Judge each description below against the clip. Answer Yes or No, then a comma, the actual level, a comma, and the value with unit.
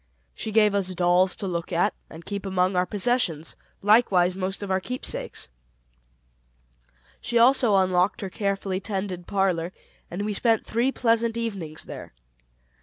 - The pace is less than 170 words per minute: Yes, average, 150 wpm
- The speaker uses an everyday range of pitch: Yes, average, 3.3 semitones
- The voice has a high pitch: Yes, high, 195 Hz